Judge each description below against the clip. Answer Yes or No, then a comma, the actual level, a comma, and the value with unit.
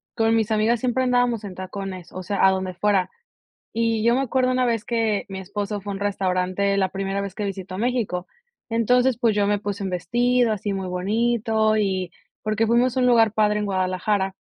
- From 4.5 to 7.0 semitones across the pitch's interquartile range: No, average, 3.2 semitones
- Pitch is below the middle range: No, high, 210 Hz